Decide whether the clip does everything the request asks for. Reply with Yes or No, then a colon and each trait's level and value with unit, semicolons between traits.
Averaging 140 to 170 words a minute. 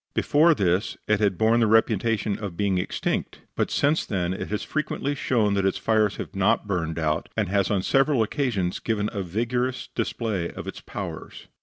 No: average, 185 wpm